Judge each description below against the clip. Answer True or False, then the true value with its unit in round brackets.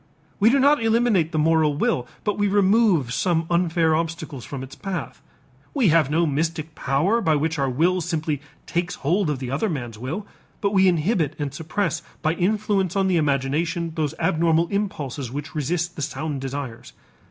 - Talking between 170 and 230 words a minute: True (175 wpm)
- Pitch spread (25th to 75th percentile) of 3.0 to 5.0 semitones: True (4.4 semitones)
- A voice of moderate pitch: True (160 Hz)